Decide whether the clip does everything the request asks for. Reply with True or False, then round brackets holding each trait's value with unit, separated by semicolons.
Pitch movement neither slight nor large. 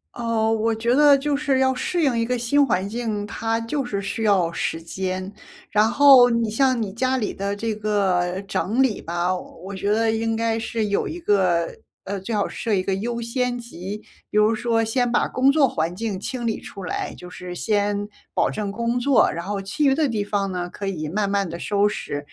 True (3.5 semitones)